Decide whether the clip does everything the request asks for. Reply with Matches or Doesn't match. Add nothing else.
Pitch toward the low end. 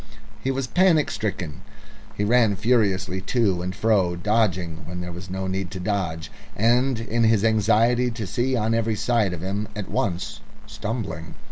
Matches